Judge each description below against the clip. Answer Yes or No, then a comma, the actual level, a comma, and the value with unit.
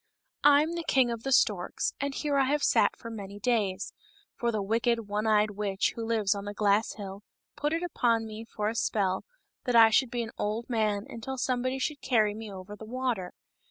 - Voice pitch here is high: Yes, high, 225 Hz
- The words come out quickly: Yes, fast, 215 wpm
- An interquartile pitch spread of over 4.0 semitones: No, average, 3.4 semitones